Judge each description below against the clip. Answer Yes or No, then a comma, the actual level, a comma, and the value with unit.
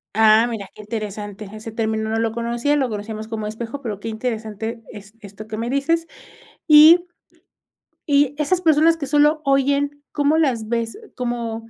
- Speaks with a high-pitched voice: Yes, high, 230 Hz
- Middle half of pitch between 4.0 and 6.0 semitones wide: Yes, average, 4.7 semitones